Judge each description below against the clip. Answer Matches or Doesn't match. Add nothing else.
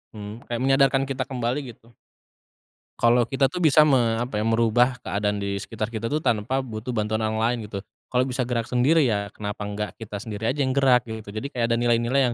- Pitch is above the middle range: Doesn't match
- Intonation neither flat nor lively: Matches